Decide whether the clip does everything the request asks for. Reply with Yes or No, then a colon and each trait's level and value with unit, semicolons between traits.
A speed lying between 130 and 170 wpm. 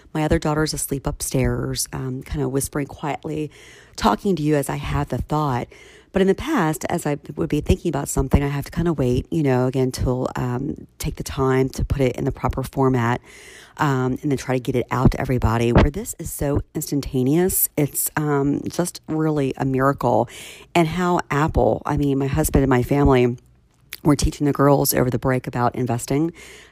No: average, 200 wpm